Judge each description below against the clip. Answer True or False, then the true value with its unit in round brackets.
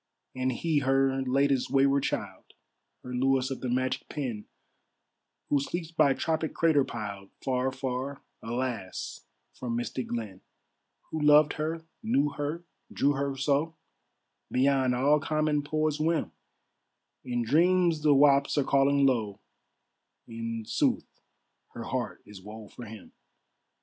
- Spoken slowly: True (130 wpm)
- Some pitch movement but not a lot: True (3.1 semitones)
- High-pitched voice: False (135 Hz)